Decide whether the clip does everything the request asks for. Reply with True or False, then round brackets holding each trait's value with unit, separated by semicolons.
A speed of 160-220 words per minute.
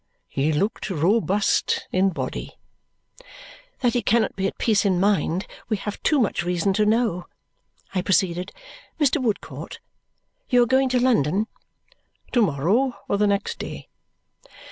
False (145 wpm)